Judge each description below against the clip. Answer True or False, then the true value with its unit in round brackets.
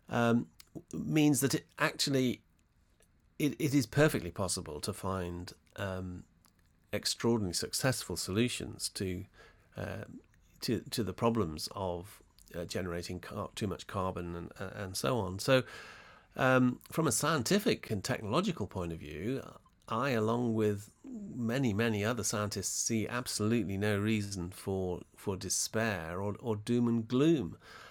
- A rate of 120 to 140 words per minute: True (135 wpm)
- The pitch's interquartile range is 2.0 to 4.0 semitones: False (5.0 semitones)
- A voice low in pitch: True (105 Hz)